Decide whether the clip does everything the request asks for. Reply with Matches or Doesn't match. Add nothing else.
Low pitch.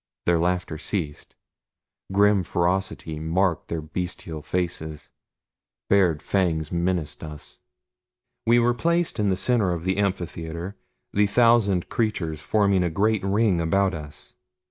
Matches